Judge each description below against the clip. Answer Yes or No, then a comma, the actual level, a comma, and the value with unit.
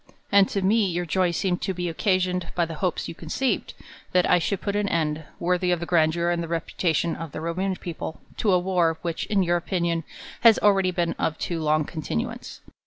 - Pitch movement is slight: Yes, narrow, 2.2 semitones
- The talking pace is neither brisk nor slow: No, fast, 210 wpm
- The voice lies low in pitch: No, medium, 175 Hz